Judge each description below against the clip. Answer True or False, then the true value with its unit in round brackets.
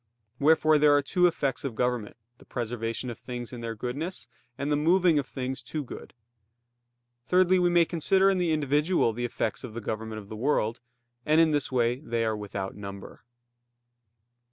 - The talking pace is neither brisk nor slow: True (180 wpm)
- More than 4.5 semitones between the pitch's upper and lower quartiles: True (5.3 semitones)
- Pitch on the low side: True (130 Hz)